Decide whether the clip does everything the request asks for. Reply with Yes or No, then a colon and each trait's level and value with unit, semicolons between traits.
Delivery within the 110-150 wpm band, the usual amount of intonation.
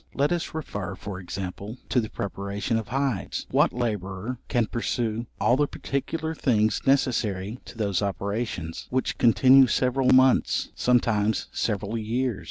Yes: average, 140 wpm; average, 4.1 semitones